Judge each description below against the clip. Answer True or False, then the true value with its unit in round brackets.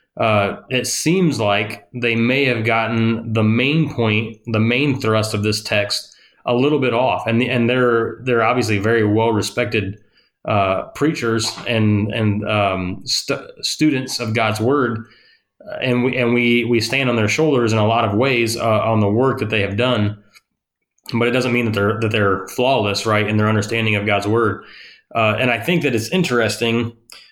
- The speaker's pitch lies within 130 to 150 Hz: False (115 Hz)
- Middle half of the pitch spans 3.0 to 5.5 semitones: False (2.4 semitones)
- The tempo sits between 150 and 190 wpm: True (185 wpm)